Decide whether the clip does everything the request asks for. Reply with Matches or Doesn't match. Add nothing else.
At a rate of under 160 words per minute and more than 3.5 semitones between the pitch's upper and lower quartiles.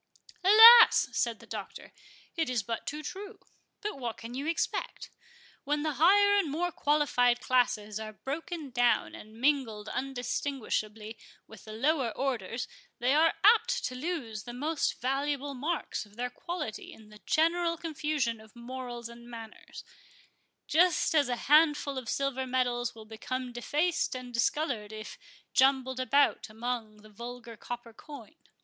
Matches